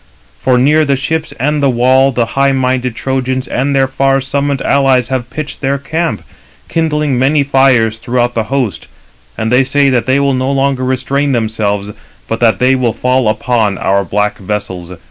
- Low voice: Yes, low, 130 Hz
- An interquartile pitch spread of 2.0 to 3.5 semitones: Yes, narrow, 2.6 semitones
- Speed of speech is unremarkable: Yes, average, 180 wpm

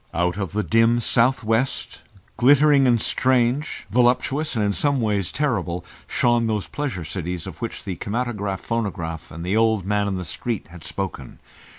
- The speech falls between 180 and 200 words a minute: No, average, 170 wpm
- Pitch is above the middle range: No, low, 110 Hz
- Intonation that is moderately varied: Yes, average, 4.9 semitones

